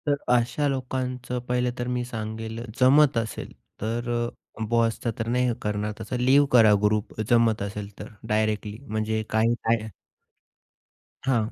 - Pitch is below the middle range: Yes, low, 115 Hz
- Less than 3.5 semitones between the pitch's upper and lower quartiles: Yes, narrow, 2.4 semitones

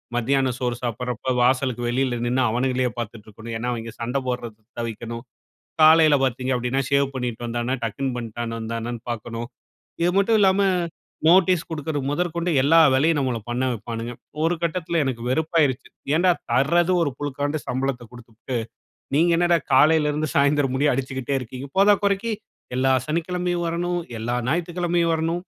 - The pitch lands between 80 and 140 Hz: Yes, low, 135 Hz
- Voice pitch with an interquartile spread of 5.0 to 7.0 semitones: Yes, average, 5.3 semitones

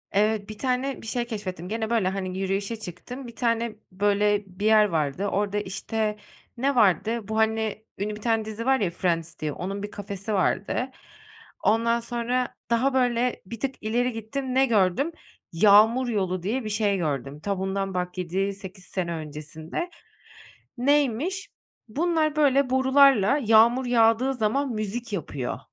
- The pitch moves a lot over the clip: No, average, 4.0 semitones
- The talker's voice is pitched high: Yes, high, 215 Hz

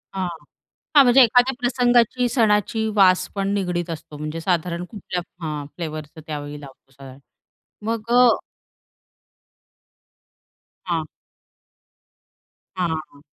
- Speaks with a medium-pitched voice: Yes, medium, 180 Hz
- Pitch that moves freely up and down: Yes, wide, 6.7 semitones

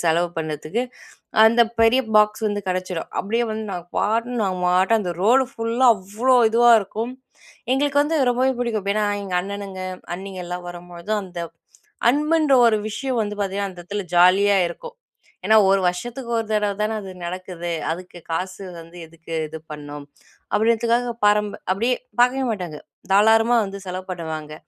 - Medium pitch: No, high, 200 Hz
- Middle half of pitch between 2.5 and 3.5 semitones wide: No, average, 4.4 semitones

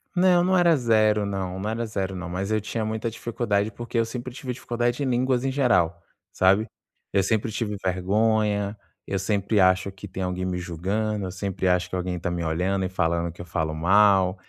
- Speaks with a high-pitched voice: No, low, 100 Hz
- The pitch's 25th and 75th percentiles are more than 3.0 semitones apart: Yes, average, 3.6 semitones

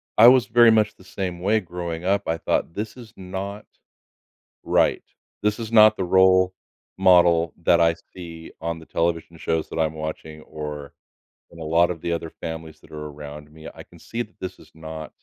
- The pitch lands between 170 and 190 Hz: No, very low, 85 Hz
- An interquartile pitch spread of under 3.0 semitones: No, average, 3.3 semitones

